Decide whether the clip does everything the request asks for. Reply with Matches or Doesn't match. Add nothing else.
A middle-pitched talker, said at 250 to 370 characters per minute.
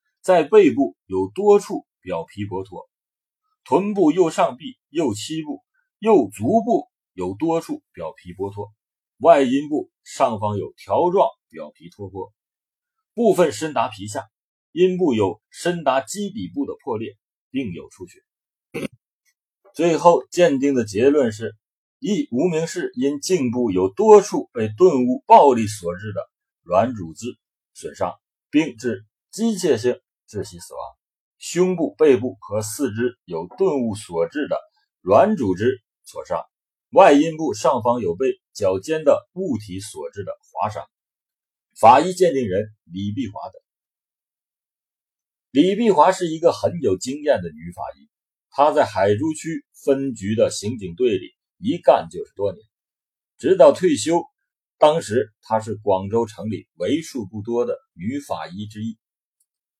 Doesn't match